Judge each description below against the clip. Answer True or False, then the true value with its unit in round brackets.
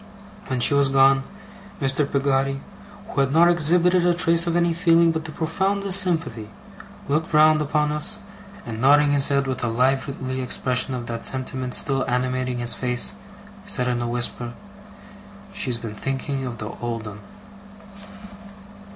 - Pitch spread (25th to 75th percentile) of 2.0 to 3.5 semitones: False (4.2 semitones)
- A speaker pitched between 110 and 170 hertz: True (135 Hz)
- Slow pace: False (155 wpm)